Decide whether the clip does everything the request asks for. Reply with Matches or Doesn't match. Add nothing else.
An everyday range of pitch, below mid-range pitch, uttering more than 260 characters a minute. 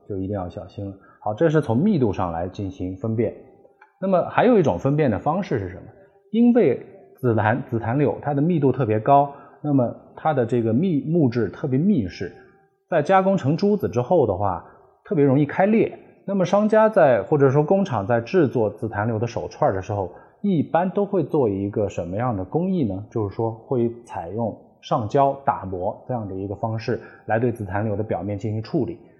Doesn't match